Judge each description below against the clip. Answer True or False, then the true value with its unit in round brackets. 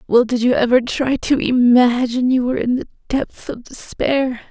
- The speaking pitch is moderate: False (250 Hz)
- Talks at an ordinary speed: True (185 wpm)